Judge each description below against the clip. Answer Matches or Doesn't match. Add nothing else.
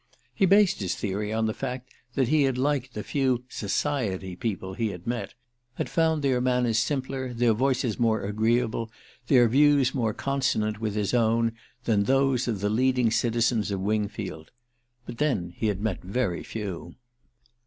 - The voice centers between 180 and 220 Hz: Doesn't match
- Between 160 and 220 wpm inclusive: Matches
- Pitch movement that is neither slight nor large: Matches